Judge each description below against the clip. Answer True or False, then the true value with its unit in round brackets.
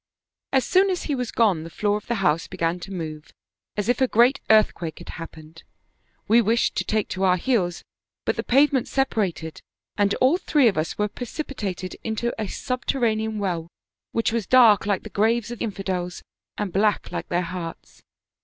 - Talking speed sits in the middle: True (180 wpm)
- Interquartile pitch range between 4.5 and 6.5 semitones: True (4.9 semitones)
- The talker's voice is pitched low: False (210 Hz)